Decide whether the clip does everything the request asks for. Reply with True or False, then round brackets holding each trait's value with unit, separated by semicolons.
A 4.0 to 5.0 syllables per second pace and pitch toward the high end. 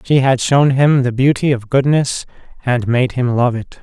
False (4.5 syllables/s; 130 Hz)